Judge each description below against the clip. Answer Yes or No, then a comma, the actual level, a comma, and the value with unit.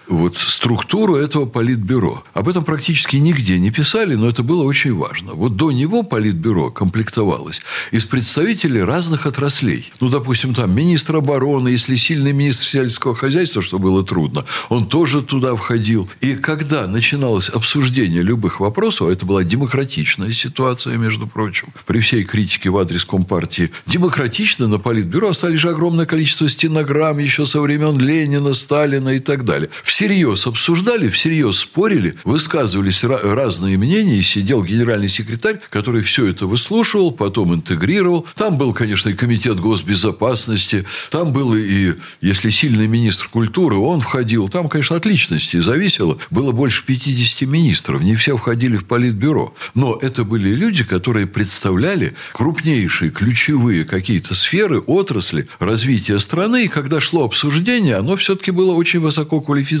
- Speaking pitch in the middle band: No, low, 130 Hz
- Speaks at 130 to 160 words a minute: Yes, average, 145 wpm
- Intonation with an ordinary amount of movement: No, wide, 6.1 semitones